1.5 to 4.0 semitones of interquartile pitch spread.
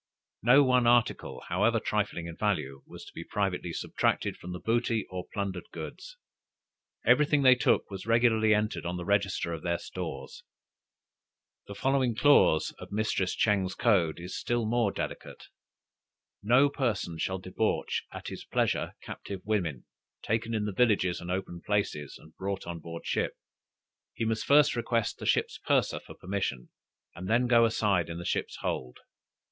No: average, 4.6 semitones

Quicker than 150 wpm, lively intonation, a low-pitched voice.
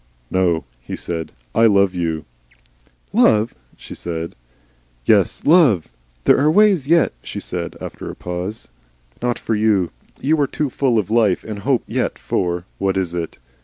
Yes: average, 160 wpm; wide, 6.5 semitones; low, 100 Hz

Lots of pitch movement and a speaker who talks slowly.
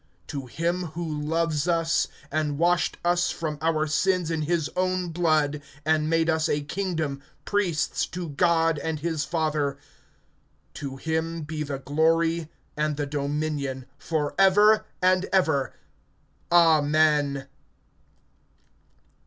No: narrow, 2.4 semitones; slow, 120 wpm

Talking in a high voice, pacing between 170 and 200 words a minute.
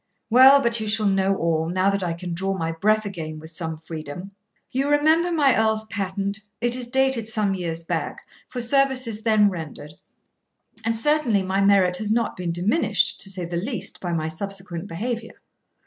Yes: high, 200 Hz; average, 180 wpm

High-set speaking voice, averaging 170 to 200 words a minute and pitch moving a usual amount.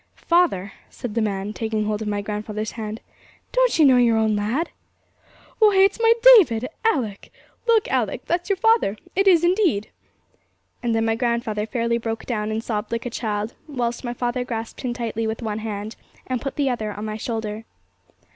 Yes: high, 230 Hz; average, 185 wpm; average, 4.3 semitones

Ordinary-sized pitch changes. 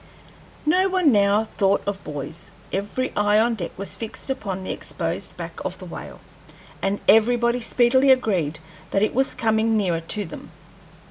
Yes: average, 3.7 semitones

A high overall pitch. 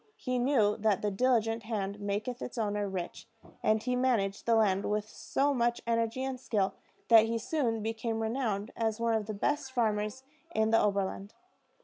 Yes: high, 225 Hz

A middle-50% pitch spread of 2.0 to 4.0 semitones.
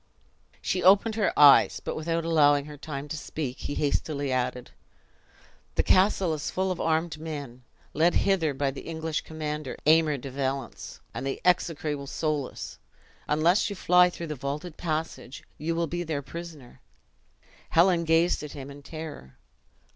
Yes: average, 2.9 semitones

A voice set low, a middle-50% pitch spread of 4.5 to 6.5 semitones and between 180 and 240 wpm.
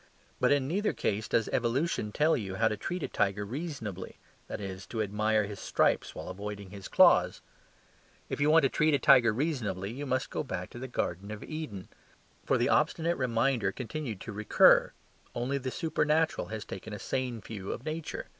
Yes: low, 115 Hz; wide, 5.6 semitones; average, 190 wpm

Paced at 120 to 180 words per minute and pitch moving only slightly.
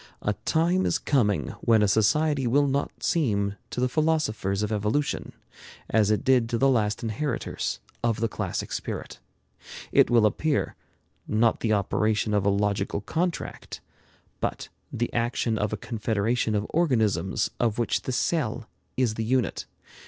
No: average, 150 wpm; average, 4.0 semitones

